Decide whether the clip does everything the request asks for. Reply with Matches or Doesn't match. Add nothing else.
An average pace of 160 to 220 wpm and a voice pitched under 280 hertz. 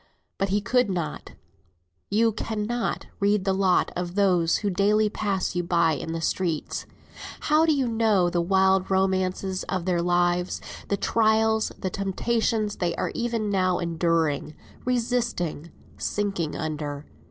Doesn't match